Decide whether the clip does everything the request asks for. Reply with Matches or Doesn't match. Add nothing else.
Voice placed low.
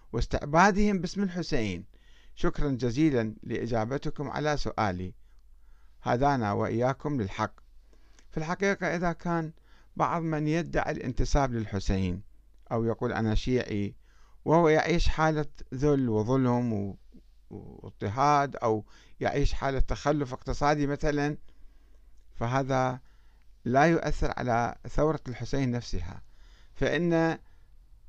Matches